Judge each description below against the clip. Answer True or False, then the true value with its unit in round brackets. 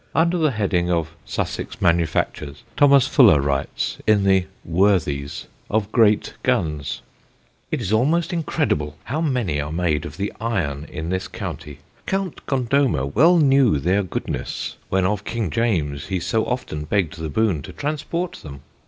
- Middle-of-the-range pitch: False (95 Hz)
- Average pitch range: False (8.7 semitones)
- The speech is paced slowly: False (155 wpm)